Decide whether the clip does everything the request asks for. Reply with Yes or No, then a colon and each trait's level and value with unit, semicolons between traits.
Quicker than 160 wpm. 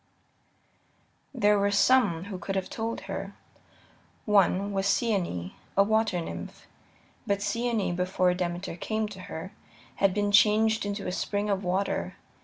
No: average, 140 wpm